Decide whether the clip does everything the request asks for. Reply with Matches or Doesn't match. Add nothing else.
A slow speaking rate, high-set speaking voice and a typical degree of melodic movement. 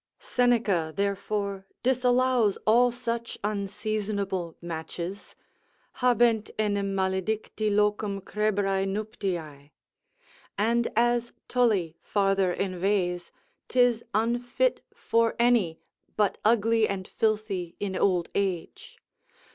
Matches